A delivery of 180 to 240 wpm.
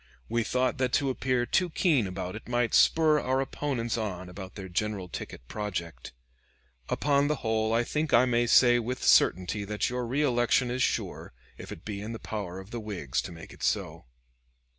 Yes: average, 190 wpm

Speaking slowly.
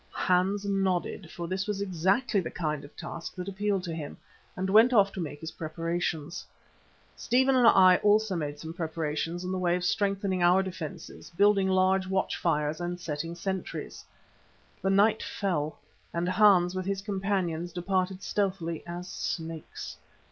No: average, 160 wpm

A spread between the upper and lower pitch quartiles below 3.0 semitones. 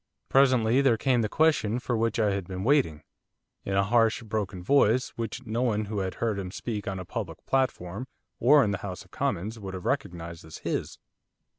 No: average, 4.2 semitones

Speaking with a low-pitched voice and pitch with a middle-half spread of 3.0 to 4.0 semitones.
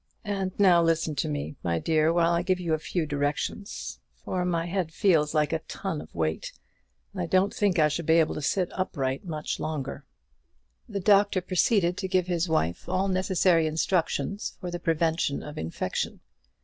No: medium, 170 Hz; average, 3.3 semitones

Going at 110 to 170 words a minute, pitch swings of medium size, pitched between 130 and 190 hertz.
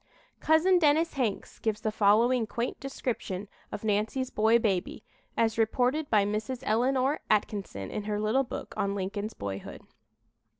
No: average, 140 wpm; average, 3.9 semitones; high, 220 Hz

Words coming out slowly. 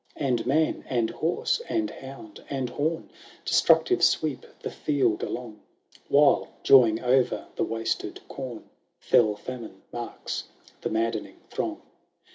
Yes: slow, 125 wpm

